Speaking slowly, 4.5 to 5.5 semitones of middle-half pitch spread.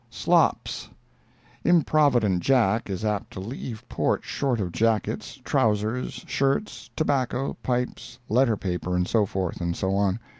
Yes: slow, 125 wpm; average, 4.8 semitones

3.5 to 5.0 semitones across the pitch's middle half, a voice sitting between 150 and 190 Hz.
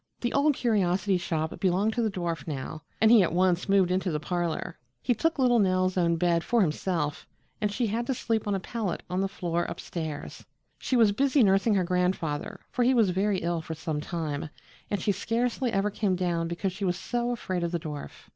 Yes: average, 4.4 semitones; medium, 185 Hz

